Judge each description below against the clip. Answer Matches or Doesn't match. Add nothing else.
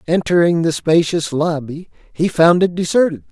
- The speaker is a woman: Doesn't match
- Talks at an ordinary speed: Matches